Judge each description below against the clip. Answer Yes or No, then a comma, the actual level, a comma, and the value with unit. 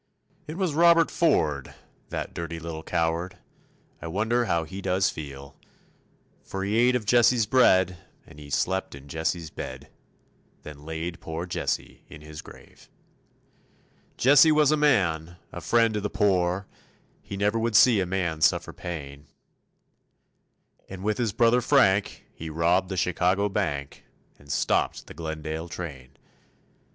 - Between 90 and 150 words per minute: Yes, average, 145 wpm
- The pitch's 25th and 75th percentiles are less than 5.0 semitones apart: No, wide, 5.4 semitones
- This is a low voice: Yes, very low, 90 Hz